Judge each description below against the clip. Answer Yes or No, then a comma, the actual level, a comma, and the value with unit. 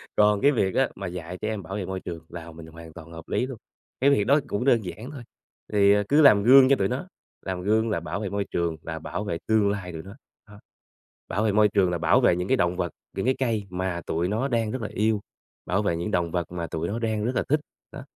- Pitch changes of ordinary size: Yes, average, 4.2 semitones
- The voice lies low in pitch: Yes, low, 100 Hz